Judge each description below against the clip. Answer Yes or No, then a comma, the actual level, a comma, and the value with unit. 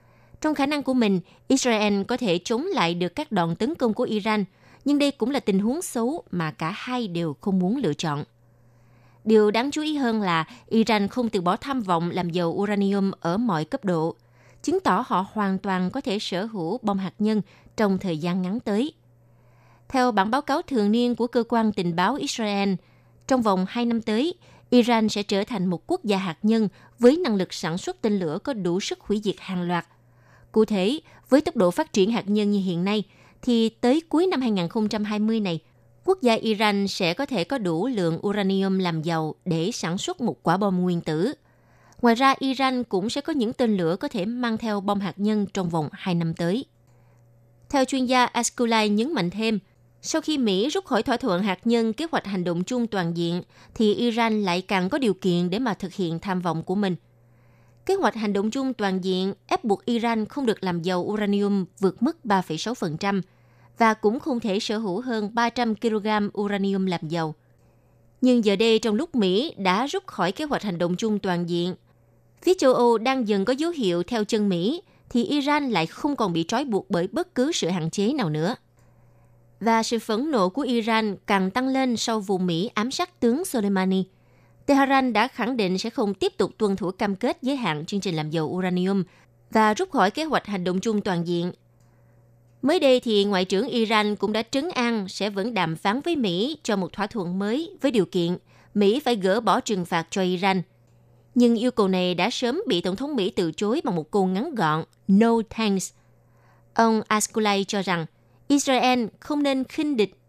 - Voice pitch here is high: Yes, high, 205 Hz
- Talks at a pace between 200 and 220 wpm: Yes, average, 210 wpm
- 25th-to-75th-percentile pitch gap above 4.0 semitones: Yes, average, 5.0 semitones